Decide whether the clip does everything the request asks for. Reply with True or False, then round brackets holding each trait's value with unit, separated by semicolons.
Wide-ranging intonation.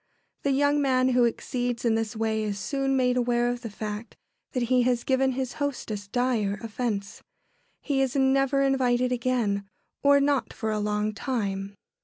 False (3.4 semitones)